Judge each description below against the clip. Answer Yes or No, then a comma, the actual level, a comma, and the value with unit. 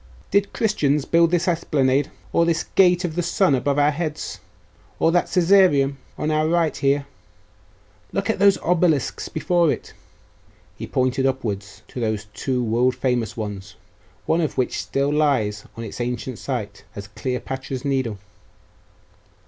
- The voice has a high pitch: No, medium, 140 Hz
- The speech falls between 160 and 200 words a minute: No, average, 150 wpm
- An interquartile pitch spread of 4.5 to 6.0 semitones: Yes, average, 5.2 semitones